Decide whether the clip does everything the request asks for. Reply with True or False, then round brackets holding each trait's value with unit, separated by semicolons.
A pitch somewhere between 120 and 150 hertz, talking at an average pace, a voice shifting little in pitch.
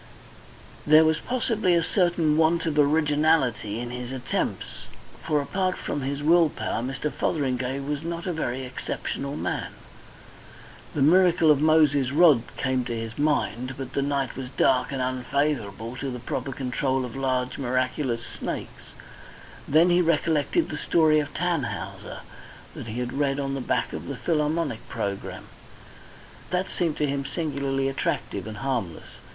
False (140 Hz; 155 wpm; 3.8 semitones)